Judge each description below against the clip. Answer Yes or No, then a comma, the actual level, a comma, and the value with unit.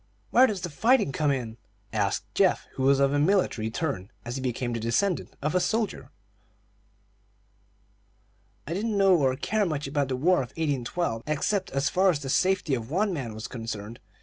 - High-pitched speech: No, medium, 140 Hz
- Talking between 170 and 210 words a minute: Yes, average, 180 wpm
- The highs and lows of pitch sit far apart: Yes, wide, 6.9 semitones